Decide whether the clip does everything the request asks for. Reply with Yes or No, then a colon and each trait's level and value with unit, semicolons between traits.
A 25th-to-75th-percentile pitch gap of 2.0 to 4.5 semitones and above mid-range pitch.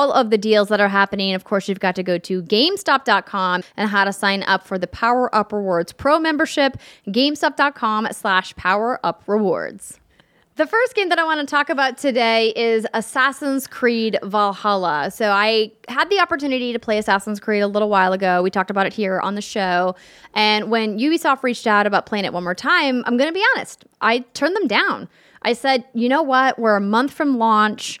No: average, 5.1 semitones; high, 220 Hz